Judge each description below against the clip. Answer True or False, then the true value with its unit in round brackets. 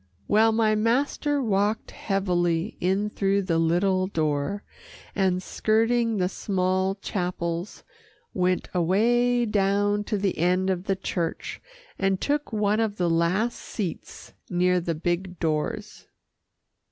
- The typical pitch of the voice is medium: False (195 Hz)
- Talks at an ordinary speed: False (125 wpm)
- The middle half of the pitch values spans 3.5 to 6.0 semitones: False (3.0 semitones)